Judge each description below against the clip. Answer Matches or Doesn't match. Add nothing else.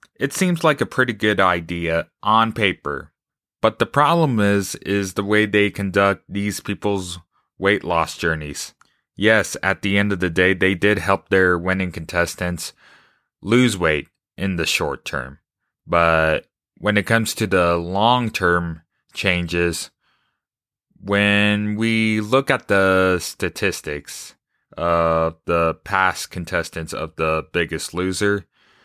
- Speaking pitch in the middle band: Doesn't match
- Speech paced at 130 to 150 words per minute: Matches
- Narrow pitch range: Doesn't match